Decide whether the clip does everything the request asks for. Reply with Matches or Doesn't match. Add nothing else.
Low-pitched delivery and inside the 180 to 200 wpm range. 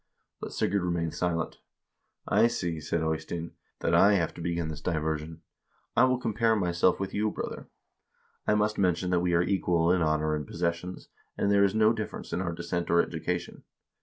Matches